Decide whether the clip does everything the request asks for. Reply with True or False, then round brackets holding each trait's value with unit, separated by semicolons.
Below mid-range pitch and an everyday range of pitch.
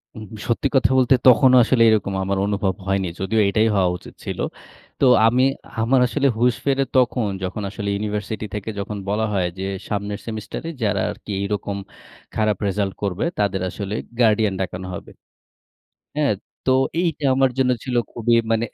True (110 Hz; 3.7 semitones)